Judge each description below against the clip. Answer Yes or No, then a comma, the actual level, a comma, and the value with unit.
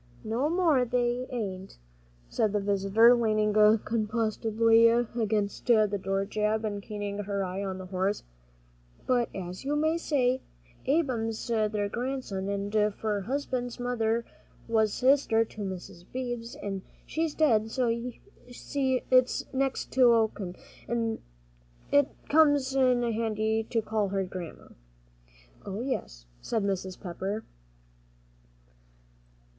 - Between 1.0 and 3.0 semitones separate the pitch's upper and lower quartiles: No, average, 3.5 semitones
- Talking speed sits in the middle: No, slow, 125 wpm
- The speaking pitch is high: Yes, high, 225 Hz